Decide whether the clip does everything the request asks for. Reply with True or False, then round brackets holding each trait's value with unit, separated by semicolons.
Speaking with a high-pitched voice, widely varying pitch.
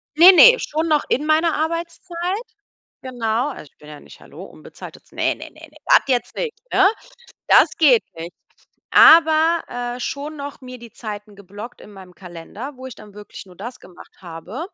True (255 Hz; 7.5 semitones)